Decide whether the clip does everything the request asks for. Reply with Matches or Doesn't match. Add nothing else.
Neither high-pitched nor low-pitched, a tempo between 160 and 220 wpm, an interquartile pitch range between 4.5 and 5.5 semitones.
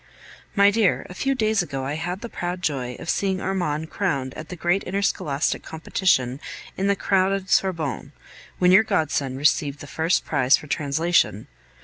Matches